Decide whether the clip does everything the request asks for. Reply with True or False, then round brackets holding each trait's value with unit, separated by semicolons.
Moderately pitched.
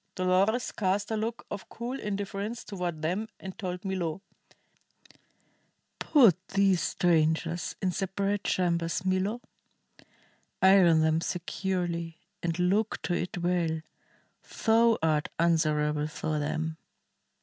True (180 Hz)